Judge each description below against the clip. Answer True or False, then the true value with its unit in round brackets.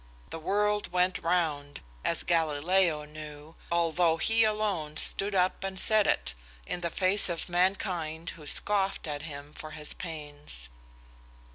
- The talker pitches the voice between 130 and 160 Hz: False (170 Hz)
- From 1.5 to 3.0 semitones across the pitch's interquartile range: False (3.9 semitones)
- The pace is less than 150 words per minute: True (140 wpm)